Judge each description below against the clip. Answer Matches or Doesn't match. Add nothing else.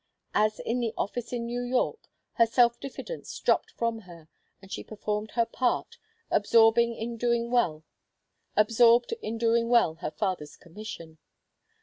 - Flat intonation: Matches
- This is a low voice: Doesn't match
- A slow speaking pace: Matches